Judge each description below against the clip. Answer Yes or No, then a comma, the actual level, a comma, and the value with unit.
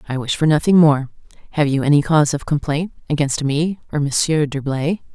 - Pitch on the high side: No, medium, 150 Hz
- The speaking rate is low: No, average, 185 wpm